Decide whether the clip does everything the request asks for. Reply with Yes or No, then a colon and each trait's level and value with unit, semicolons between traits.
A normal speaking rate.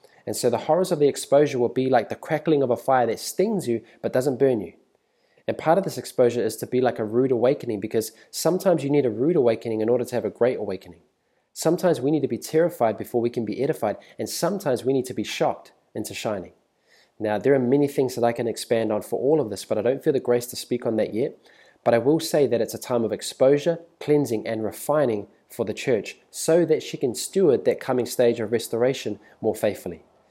No: fast, 240 wpm